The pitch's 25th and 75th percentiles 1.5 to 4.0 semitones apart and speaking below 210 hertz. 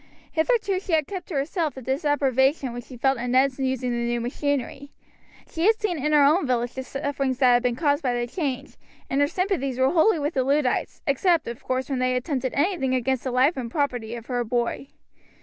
No: average, 3.1 semitones; very high, 270 Hz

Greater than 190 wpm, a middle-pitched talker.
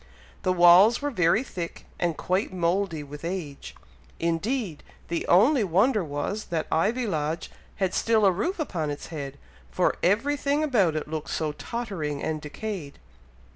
No: average, 155 wpm; medium, 180 Hz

